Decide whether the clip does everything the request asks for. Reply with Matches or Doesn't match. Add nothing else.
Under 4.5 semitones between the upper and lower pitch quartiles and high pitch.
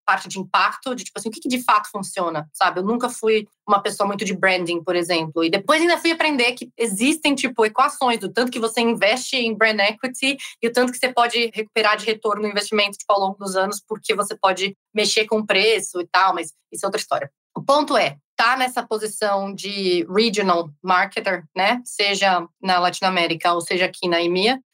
Matches